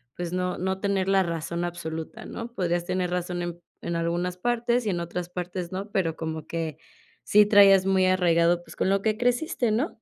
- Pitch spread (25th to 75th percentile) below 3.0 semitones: Yes, narrow, 2.5 semitones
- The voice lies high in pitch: No, medium, 180 Hz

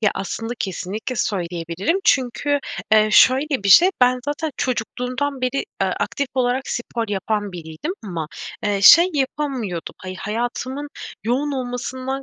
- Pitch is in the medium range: No, high, 245 Hz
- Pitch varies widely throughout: No, average, 4.8 semitones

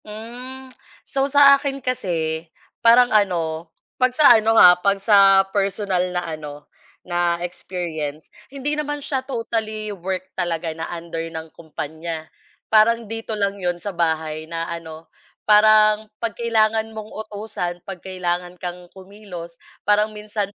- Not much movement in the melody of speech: No, average, 4.4 semitones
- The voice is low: No, high, 195 Hz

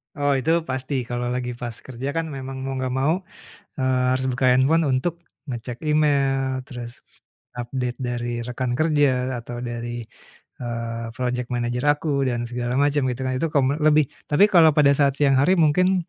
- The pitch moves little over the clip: No, average, 3.0 semitones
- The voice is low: Yes, low, 130 Hz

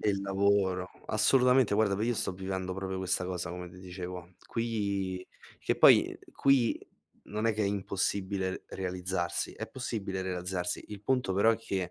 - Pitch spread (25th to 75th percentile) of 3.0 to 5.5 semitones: No, narrow, 2.4 semitones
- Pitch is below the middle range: Yes, very low, 95 Hz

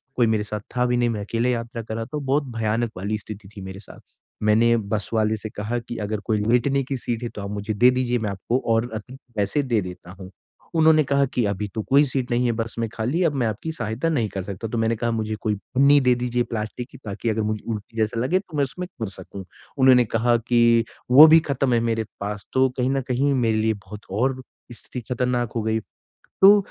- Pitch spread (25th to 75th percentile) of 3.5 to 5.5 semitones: No, average, 2.8 semitones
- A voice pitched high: No, low, 115 Hz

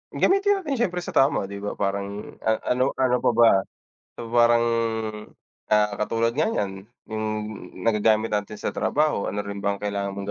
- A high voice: No, low, 110 Hz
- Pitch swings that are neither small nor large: Yes, average, 3.9 semitones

